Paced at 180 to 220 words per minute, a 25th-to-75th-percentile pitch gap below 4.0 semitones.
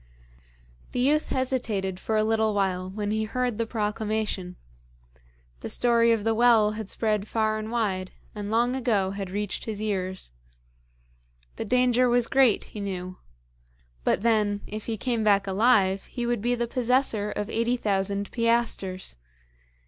No: average, 155 wpm; average, 2.9 semitones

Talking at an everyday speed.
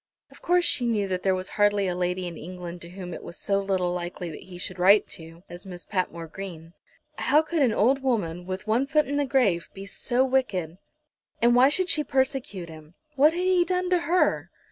No: fast, 220 wpm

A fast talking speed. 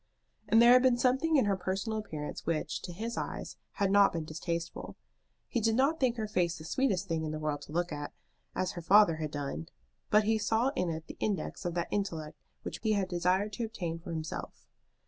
Yes: fast, 220 wpm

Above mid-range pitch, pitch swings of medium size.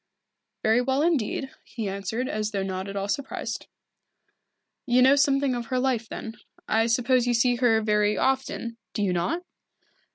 Yes: high, 235 Hz; average, 3.8 semitones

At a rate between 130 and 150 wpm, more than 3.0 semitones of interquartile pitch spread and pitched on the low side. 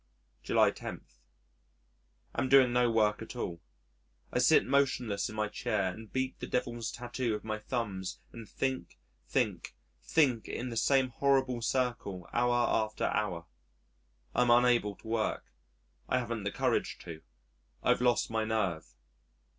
No: average, 145 wpm; average, 2.7 semitones; low, 115 Hz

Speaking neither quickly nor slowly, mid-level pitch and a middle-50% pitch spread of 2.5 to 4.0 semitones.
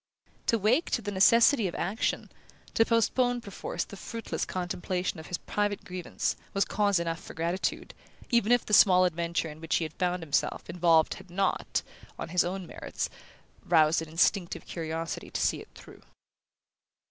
Yes: average, 165 wpm; medium, 180 Hz; average, 3.6 semitones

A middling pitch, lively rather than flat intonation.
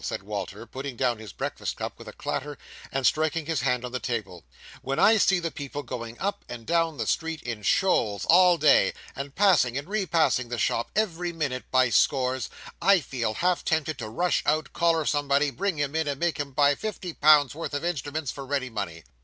No: medium, 145 Hz; average, 4.8 semitones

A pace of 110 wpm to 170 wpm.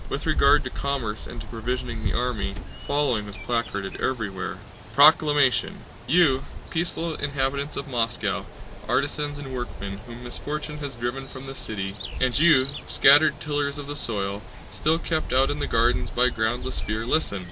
Yes: average, 160 wpm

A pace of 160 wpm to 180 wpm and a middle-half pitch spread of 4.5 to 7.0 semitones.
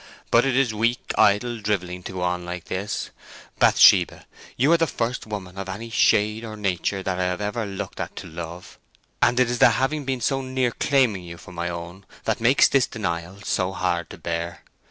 No: fast, 205 wpm; average, 5.1 semitones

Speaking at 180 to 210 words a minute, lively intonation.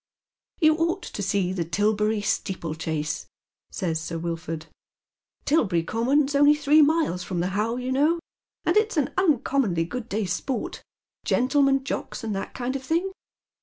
No: average, 150 wpm; wide, 8.1 semitones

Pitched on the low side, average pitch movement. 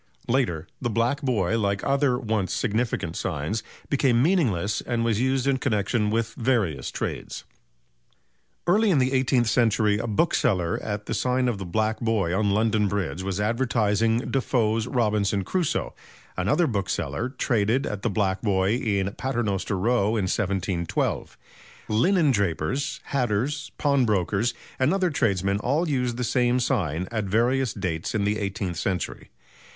Yes: low, 110 Hz; average, 4.2 semitones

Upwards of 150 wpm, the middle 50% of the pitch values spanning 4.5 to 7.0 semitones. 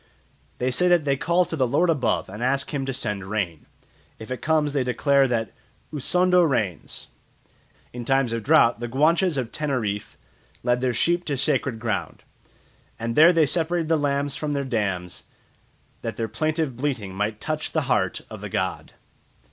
Yes: average, 175 wpm; average, 5.1 semitones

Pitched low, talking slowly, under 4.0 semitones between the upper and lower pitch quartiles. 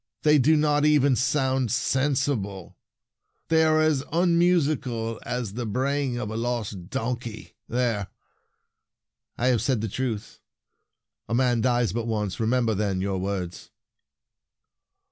No: low, 125 Hz; slow, 130 wpm; average, 4.3 semitones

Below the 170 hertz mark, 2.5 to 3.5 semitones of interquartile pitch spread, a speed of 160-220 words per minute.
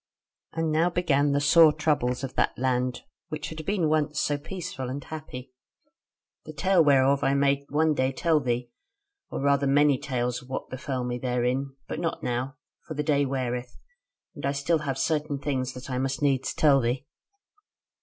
Yes: medium, 140 Hz; average, 2.9 semitones; average, 180 wpm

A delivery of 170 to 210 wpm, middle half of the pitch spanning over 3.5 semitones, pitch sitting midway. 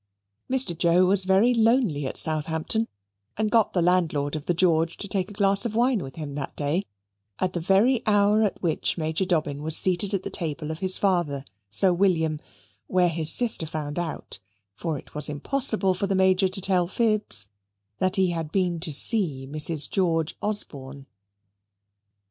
Yes: average, 180 wpm; average, 4.1 semitones; medium, 180 Hz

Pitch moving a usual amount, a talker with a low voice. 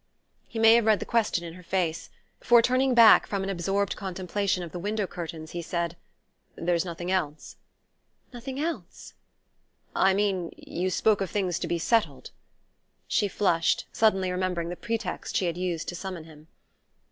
No: average, 3.5 semitones; medium, 185 Hz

